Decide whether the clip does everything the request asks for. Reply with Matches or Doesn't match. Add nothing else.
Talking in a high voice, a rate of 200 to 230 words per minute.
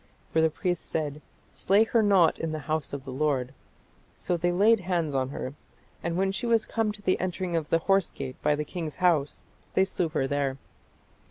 Doesn't match